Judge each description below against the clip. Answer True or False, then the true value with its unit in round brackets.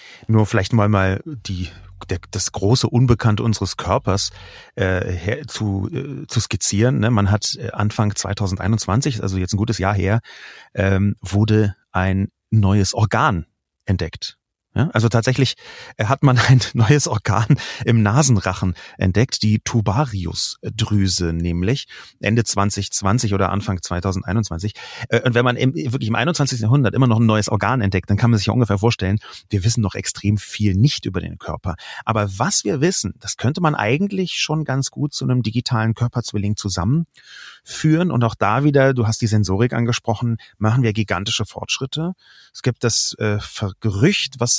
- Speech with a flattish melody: False (3.6 semitones)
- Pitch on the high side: False (110 Hz)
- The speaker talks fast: False (160 wpm)